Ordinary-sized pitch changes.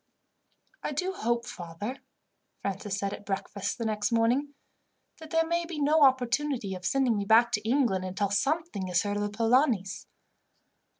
No: wide, 5.7 semitones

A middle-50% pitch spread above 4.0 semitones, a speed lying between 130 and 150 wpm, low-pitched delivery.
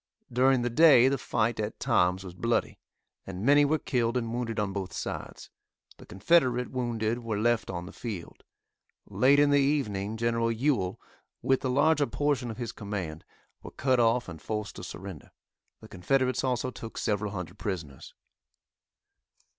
No: average, 4.4 semitones; average, 160 wpm; low, 115 Hz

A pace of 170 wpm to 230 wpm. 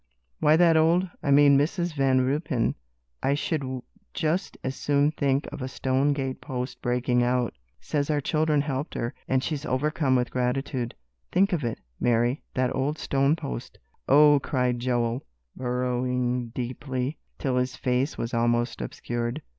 No: average, 155 wpm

